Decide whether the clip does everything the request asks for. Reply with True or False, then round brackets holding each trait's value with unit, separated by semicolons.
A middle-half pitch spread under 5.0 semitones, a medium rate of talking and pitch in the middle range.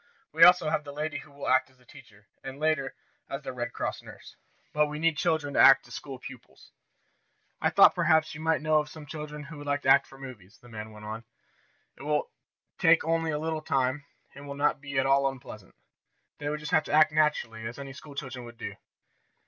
False (2.7 semitones; 235 wpm; 145 Hz)